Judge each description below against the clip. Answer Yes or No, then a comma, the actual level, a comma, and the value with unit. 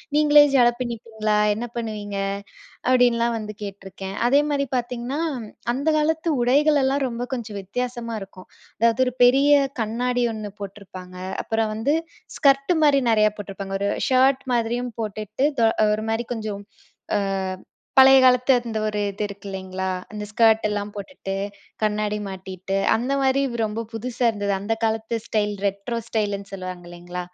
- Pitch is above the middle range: Yes, high, 225 Hz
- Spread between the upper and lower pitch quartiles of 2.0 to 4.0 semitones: Yes, average, 3.7 semitones